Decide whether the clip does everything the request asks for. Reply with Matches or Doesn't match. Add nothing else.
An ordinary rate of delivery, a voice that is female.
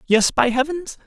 Matches